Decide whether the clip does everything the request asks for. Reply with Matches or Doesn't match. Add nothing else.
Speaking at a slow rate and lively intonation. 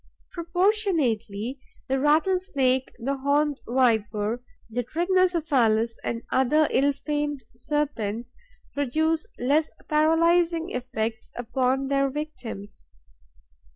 Doesn't match